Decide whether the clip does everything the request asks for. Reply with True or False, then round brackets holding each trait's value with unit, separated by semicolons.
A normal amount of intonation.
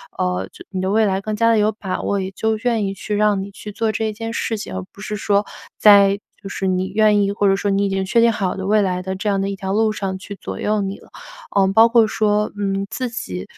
False (1.9 semitones)